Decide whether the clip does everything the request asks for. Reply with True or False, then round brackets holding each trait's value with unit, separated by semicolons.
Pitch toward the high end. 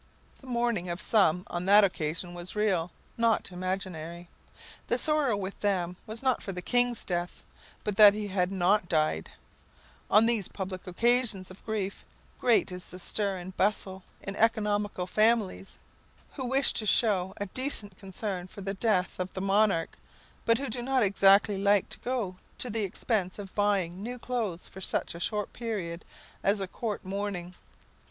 True (200 Hz)